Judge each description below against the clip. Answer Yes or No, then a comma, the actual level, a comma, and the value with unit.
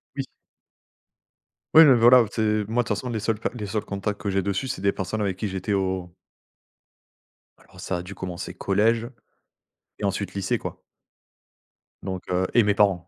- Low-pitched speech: Yes, low, 100 Hz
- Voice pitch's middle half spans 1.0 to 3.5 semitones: Yes, average, 2.7 semitones